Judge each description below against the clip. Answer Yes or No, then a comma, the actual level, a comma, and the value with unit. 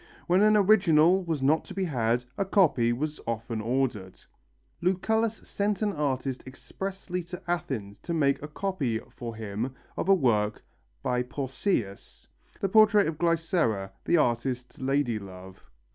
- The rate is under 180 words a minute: Yes, average, 145 wpm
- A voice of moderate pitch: Yes, medium, 145 Hz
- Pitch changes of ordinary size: No, wide, 7.7 semitones